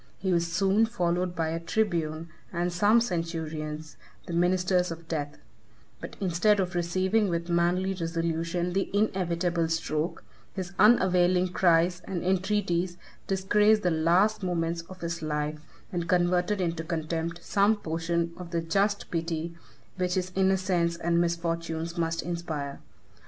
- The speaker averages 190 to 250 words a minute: No, slow, 135 wpm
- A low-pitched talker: No, medium, 175 Hz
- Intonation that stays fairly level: Yes, narrow, 2.0 semitones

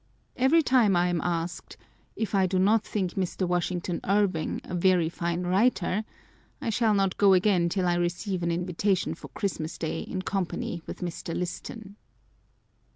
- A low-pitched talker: No, medium, 185 Hz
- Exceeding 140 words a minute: Yes, average, 170 wpm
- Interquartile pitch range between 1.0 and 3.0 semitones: Yes, narrow, 2.6 semitones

